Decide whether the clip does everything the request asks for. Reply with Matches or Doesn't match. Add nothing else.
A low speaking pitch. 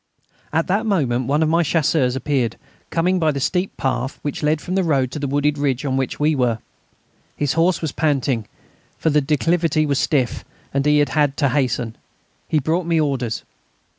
Doesn't match